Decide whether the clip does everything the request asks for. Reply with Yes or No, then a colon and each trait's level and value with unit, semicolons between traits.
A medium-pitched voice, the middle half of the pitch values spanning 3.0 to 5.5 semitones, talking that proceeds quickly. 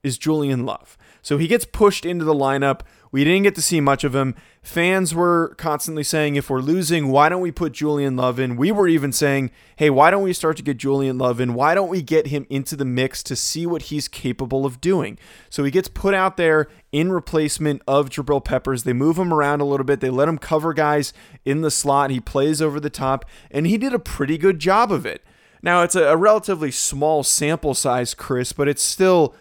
Yes: medium, 150 Hz; average, 3.5 semitones; fast, 230 wpm